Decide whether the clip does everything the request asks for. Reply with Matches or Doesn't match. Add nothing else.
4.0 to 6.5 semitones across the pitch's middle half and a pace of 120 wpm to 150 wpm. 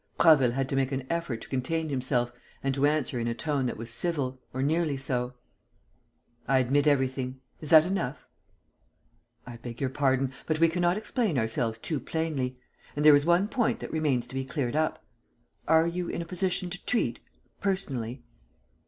Doesn't match